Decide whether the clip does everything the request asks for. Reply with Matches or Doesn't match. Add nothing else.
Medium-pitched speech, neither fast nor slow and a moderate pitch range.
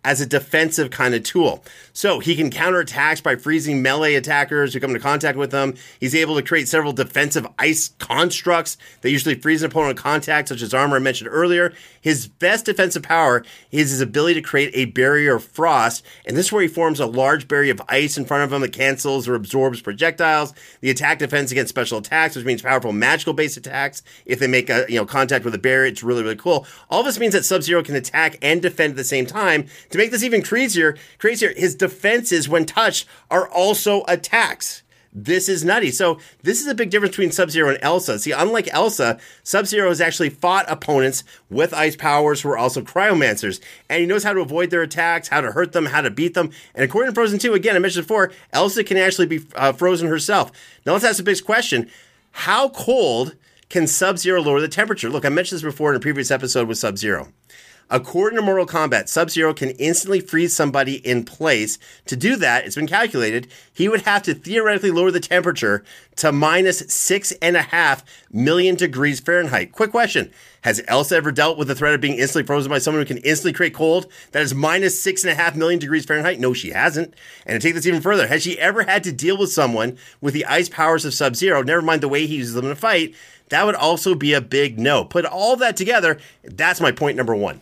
Doesn't match